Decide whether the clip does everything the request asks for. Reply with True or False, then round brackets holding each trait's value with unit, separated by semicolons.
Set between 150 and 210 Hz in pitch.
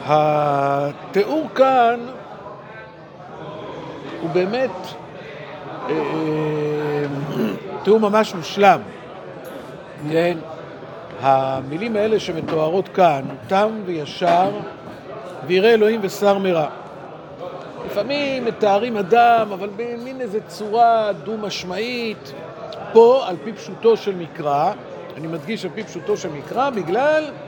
True (190 Hz)